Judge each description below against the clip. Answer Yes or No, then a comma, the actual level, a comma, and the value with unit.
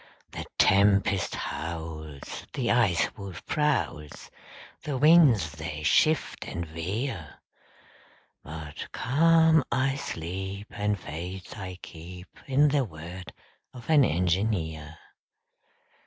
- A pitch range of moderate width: No, wide, 7.9 semitones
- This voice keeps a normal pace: No, slow, 100 wpm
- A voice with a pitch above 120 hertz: No, very low, 95 Hz